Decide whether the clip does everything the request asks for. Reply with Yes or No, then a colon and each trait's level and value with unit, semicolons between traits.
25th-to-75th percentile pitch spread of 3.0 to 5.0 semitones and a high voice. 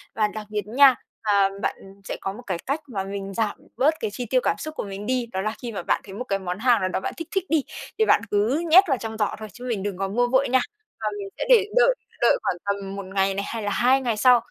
Yes: average, 4.4 semitones; high, 215 Hz